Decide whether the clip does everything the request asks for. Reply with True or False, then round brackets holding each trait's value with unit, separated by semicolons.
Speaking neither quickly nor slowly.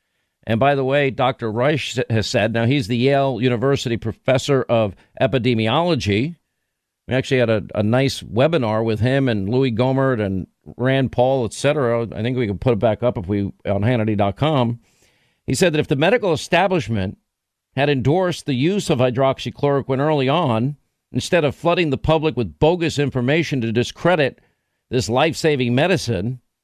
True (160 wpm)